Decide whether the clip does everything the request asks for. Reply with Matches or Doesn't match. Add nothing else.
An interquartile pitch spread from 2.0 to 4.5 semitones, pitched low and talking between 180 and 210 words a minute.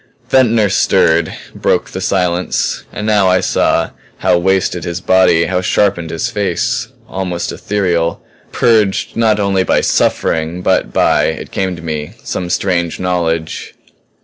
Doesn't match